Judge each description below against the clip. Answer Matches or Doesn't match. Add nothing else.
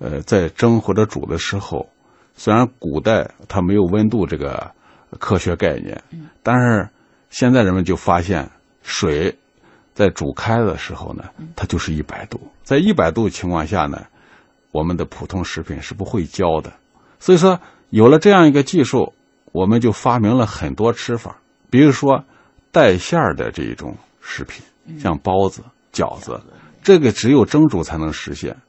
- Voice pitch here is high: Doesn't match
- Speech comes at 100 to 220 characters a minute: Doesn't match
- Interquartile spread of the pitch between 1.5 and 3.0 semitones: Doesn't match